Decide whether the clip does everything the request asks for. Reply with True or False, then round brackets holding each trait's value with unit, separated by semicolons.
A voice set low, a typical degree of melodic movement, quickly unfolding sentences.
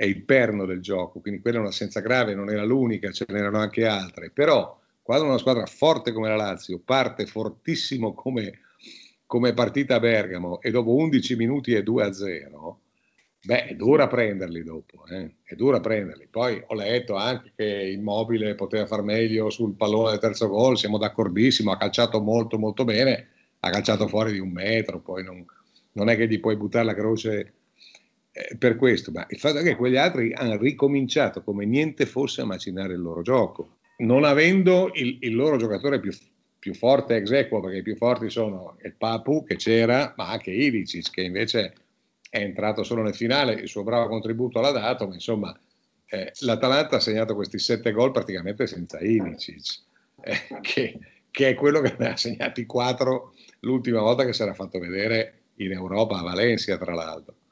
True (110 Hz; 3.3 semitones; 185 wpm)